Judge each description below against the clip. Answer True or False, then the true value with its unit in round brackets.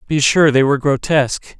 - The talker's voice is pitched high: False (140 Hz)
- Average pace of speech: True (190 wpm)